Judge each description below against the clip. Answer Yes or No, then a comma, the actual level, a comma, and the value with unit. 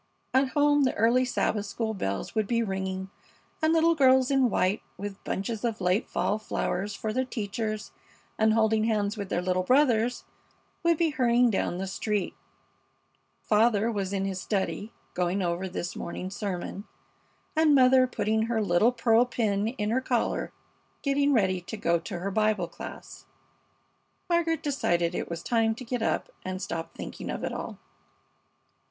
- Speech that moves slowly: No, average, 165 wpm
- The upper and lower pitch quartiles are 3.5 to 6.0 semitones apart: Yes, average, 4.4 semitones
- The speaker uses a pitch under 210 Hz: No, high, 220 Hz